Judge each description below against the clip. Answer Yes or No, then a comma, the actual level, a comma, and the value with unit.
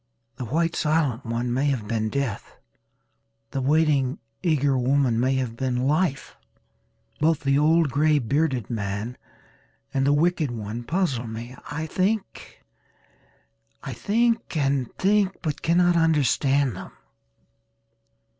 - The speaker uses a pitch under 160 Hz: Yes, medium, 140 Hz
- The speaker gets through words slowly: Yes, slow, 115 wpm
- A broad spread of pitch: No, average, 4.6 semitones